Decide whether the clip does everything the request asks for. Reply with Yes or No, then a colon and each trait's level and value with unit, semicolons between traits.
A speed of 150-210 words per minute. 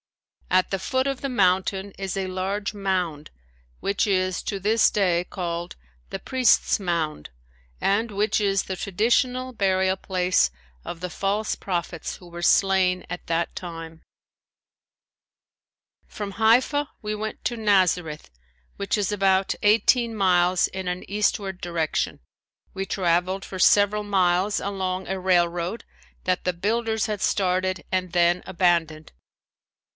No: slow, 135 wpm